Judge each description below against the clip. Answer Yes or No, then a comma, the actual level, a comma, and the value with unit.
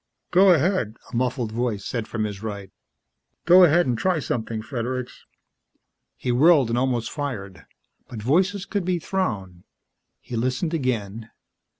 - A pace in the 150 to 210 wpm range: No, average, 140 wpm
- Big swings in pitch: Yes, wide, 6.9 semitones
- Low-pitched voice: Yes, low, 125 Hz